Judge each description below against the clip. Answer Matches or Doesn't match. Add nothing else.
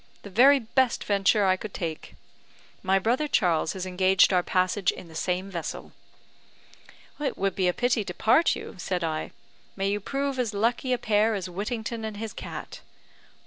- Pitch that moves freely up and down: Doesn't match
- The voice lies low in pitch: Doesn't match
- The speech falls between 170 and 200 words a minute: Matches